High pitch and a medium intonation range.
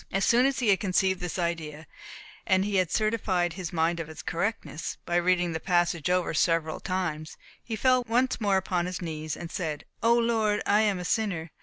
No: medium, 180 Hz; average, 3.8 semitones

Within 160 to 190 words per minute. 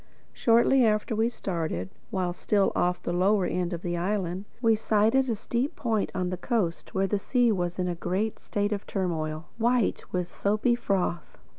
Yes: average, 180 wpm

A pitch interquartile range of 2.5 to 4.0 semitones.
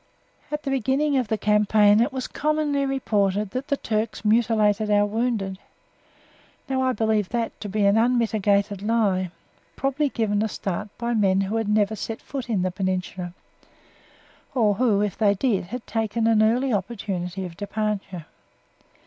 Yes: average, 3.0 semitones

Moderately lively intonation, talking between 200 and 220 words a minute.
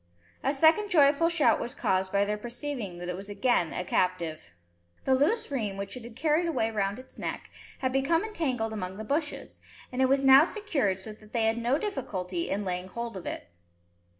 No: wide, 6.4 semitones; fast, 205 wpm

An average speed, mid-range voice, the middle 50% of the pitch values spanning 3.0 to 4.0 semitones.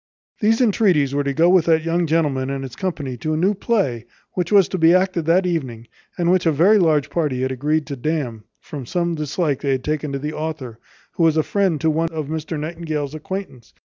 No: fast, 225 wpm; medium, 155 Hz; average, 3.7 semitones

